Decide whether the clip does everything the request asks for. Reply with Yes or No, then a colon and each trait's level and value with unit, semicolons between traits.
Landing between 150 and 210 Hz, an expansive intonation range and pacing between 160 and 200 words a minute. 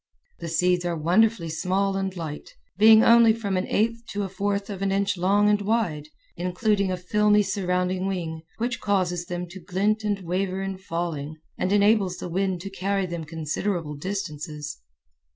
No: high, 190 Hz; narrow, 2.6 semitones; average, 170 wpm